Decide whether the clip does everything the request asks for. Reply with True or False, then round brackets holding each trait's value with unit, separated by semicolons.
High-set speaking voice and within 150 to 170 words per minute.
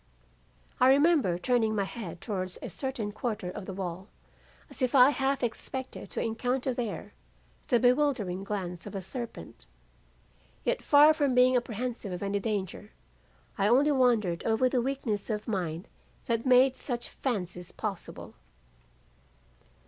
False (230 Hz; 140 wpm)